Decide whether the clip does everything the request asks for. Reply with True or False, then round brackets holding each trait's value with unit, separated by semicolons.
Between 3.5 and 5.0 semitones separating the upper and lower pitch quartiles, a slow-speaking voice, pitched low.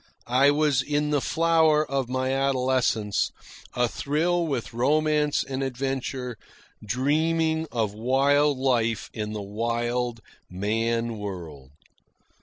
True (4.2 semitones; 110 wpm; 130 Hz)